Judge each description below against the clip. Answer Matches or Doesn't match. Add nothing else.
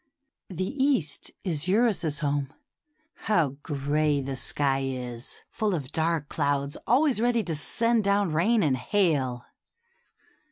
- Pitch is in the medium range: Matches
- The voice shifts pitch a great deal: Matches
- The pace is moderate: Doesn't match